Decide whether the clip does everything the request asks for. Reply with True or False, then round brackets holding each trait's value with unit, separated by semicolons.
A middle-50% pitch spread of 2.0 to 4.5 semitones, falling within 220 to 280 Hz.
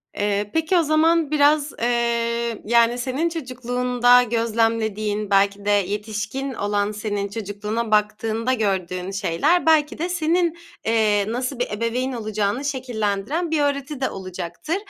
False (5.0 semitones; 230 Hz)